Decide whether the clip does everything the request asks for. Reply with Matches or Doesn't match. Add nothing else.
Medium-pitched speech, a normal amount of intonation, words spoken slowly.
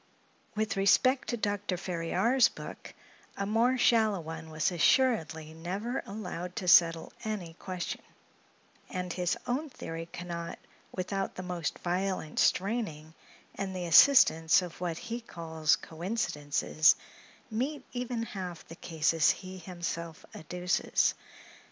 Matches